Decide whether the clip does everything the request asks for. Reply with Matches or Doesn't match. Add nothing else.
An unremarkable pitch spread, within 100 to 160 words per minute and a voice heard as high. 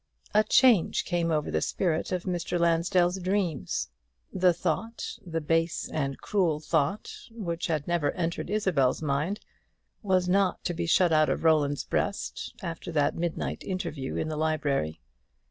Doesn't match